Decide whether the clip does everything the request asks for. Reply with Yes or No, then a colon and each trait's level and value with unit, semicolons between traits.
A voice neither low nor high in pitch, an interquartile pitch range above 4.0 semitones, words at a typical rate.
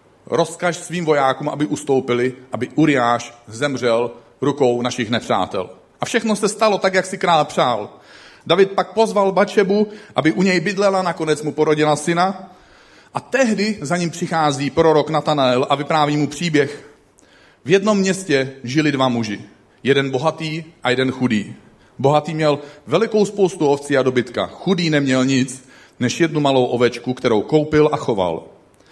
Yes: medium, 150 Hz; wide, 5.4 semitones; average, 150 wpm